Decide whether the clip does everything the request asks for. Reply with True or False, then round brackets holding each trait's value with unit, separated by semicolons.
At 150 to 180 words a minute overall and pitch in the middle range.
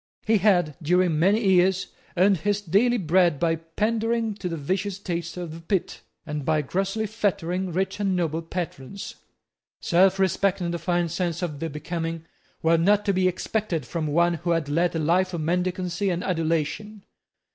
True (170 wpm; 180 Hz)